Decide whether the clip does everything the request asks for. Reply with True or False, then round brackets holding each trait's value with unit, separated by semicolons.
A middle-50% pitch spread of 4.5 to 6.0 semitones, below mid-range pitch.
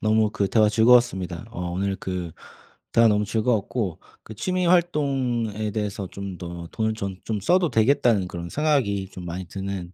False (3.9 semitones; 105 Hz)